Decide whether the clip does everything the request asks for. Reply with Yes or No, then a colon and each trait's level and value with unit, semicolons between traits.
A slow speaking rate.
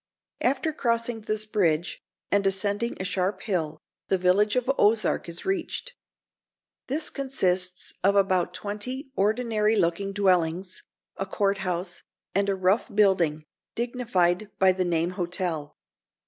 Yes: slow, 130 wpm